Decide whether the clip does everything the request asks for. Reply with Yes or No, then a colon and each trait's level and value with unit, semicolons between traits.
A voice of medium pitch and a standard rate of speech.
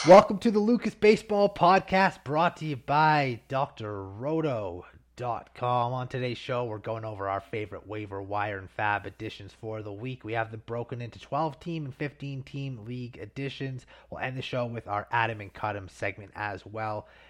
No: low, 120 Hz; average, 175 wpm